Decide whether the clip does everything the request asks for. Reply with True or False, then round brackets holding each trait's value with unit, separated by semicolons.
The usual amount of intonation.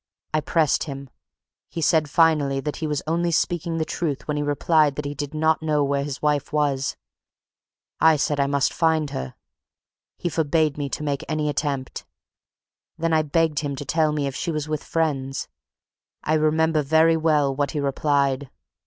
False (2.1 semitones)